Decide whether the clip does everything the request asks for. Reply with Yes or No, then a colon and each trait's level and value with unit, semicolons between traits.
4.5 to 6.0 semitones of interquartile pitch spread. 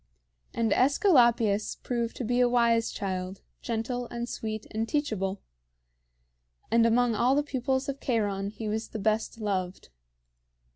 No: narrow, 2.6 semitones